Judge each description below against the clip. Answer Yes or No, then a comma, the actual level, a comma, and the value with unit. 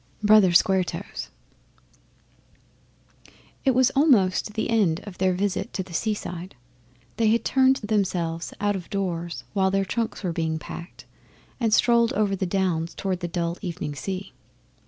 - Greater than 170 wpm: No, average, 150 wpm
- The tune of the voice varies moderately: Yes, average, 3.6 semitones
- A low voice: No, high, 190 Hz